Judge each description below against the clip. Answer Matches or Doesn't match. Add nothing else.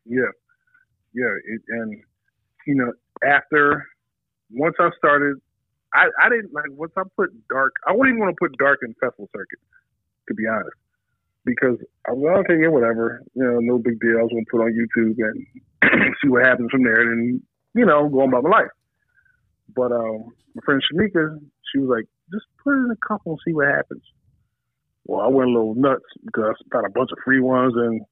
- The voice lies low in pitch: Matches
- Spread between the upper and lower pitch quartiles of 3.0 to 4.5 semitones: Doesn't match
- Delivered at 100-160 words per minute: Doesn't match